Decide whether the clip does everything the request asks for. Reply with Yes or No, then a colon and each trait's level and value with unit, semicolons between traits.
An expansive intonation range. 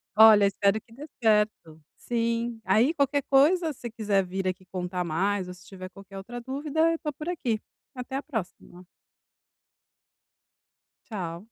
Yes: wide, 5.8 semitones